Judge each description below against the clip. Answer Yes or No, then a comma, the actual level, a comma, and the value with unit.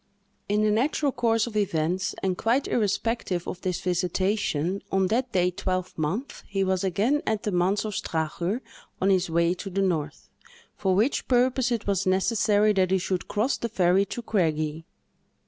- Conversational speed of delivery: Yes, average, 170 wpm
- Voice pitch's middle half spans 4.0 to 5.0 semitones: No, average, 3.5 semitones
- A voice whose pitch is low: No, high, 195 Hz